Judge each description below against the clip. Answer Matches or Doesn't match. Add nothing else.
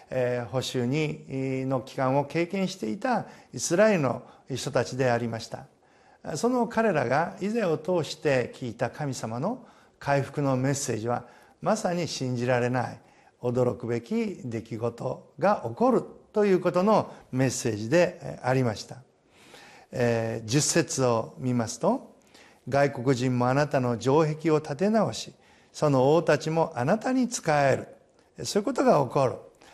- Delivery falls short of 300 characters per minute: Matches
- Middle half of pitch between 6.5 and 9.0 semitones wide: Doesn't match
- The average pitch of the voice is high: Doesn't match